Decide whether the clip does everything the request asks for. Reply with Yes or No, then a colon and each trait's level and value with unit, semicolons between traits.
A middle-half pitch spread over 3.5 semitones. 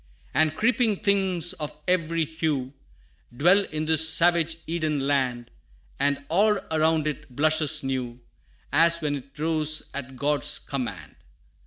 No: average, 2.7 semitones